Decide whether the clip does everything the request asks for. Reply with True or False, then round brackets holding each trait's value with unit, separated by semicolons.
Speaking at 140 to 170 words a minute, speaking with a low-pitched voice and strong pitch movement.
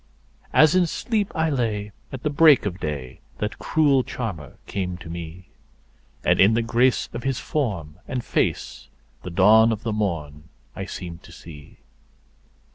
True (155 wpm; 105 Hz; 7.1 semitones)